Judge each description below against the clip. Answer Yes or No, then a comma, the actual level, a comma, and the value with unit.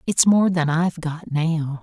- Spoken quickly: No, average, 195 wpm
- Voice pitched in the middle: Yes, medium, 165 Hz